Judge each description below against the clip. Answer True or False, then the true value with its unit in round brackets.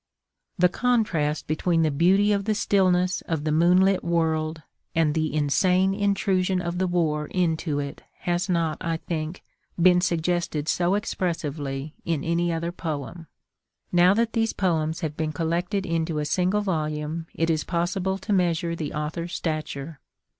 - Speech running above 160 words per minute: False (155 wpm)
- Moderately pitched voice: True (170 Hz)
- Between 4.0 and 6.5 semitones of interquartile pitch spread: False (2.7 semitones)